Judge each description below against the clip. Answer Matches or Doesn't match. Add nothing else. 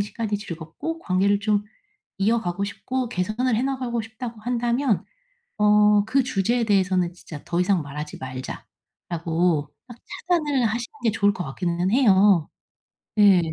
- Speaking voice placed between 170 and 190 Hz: Doesn't match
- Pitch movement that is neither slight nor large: Matches